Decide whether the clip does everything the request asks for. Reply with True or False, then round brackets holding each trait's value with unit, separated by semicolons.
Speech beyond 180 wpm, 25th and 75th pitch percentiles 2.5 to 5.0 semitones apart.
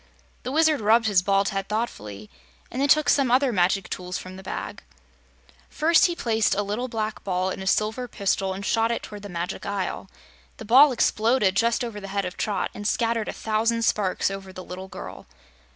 True (200 wpm; 3.5 semitones)